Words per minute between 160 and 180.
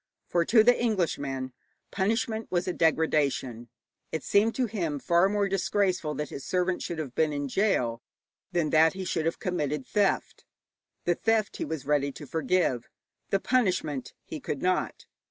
Yes: average, 165 wpm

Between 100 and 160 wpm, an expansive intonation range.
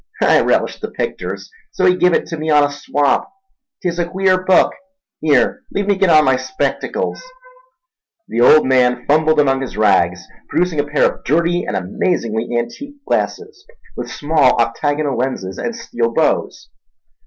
Yes: average, 155 wpm; wide, 6.2 semitones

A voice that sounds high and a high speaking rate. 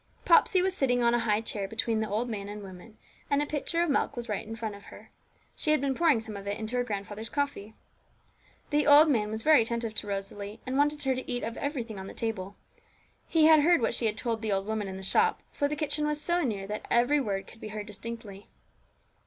Yes: high, 230 Hz; fast, 245 wpm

